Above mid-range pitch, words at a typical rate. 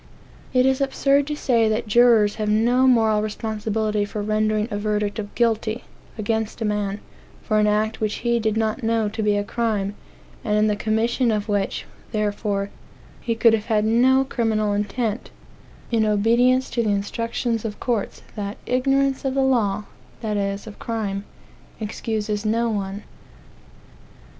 Yes: high, 220 Hz; average, 160 wpm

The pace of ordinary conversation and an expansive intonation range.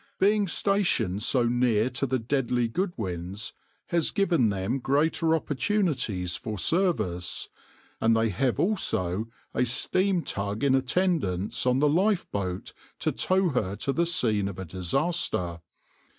No: slow, 130 wpm; wide, 9.0 semitones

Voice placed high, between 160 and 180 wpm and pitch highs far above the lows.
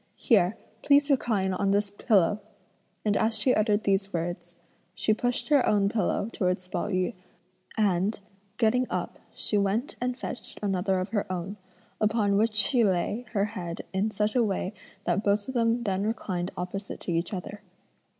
No: high, 205 Hz; average, 170 wpm; average, 2.9 semitones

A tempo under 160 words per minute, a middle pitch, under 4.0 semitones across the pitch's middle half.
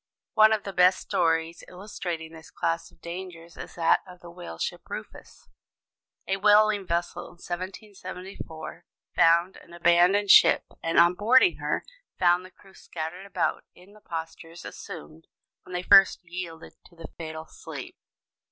Yes: average, 150 wpm; medium, 175 Hz; narrow, 2.5 semitones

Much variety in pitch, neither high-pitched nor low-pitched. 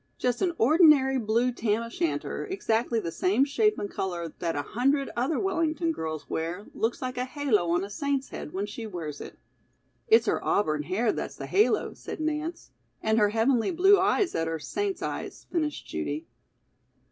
No: wide, 8.4 semitones; high, 240 Hz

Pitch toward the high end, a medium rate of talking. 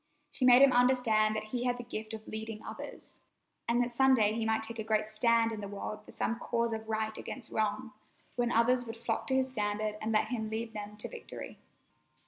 No: high, 225 Hz; fast, 225 wpm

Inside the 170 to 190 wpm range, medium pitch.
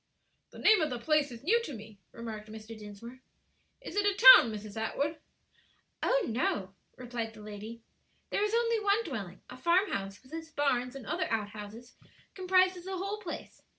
No: average, 180 wpm; very high, 255 Hz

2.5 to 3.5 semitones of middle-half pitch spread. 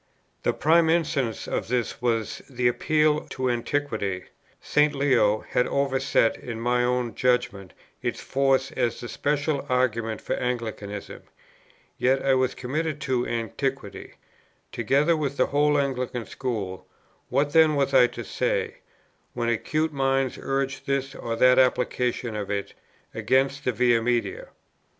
Yes: average, 2.8 semitones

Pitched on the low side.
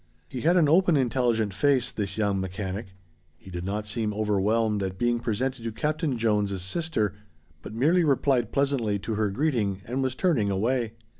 Yes: low, 115 Hz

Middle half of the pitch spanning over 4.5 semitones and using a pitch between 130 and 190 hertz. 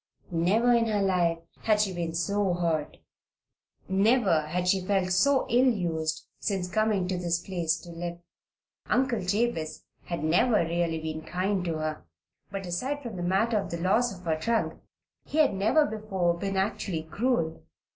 No: average, 4.1 semitones; medium, 185 Hz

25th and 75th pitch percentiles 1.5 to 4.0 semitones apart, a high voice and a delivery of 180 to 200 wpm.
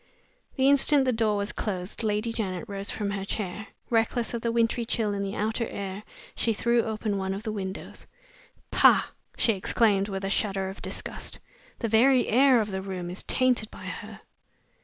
Yes: average, 2.9 semitones; high, 215 Hz; average, 185 wpm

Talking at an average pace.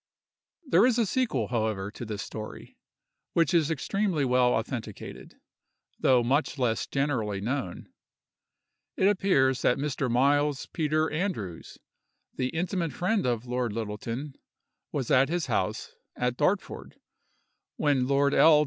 No: slow, 130 wpm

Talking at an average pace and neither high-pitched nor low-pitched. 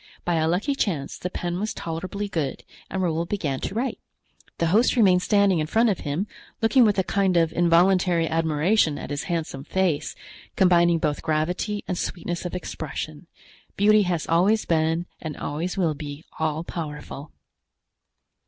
Yes: average, 160 wpm; medium, 175 Hz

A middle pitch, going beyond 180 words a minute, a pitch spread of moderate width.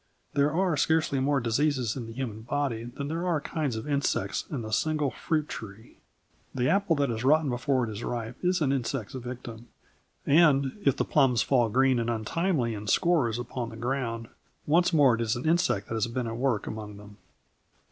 No: low, 130 Hz; average, 200 wpm; average, 4.3 semitones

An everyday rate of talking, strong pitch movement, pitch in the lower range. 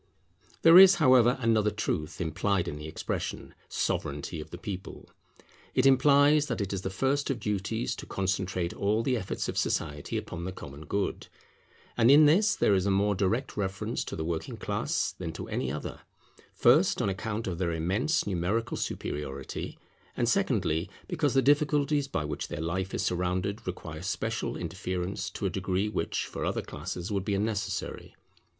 Yes: average, 170 wpm; wide, 5.9 semitones; low, 100 Hz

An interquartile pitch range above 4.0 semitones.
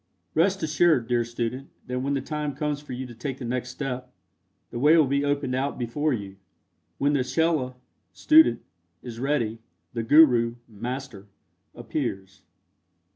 No: average, 3.5 semitones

